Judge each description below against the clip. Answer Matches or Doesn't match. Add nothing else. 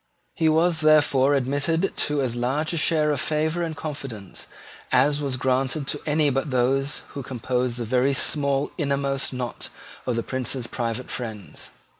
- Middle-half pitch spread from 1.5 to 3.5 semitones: Matches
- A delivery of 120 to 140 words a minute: Doesn't match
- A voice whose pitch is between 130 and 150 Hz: Matches